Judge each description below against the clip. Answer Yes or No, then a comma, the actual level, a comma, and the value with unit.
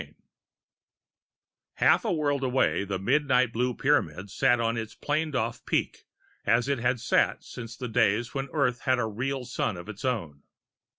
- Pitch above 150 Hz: No, low, 125 Hz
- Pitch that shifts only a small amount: No, average, 3.3 semitones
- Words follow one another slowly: No, average, 170 wpm